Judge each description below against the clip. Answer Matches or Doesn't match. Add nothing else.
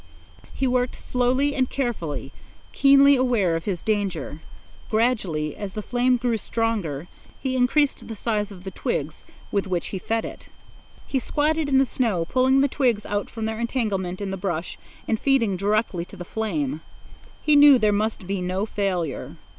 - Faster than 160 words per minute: Matches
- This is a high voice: Matches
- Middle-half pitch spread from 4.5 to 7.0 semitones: Matches